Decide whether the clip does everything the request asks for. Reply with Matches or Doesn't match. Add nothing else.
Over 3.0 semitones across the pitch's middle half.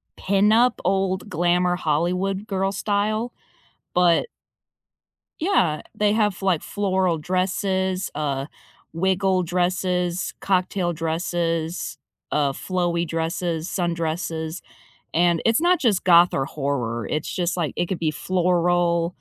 Doesn't match